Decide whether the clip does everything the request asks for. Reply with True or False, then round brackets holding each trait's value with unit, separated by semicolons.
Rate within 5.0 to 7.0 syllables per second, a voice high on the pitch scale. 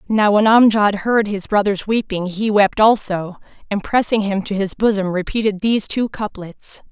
False (4.7 syllables/s; 205 Hz)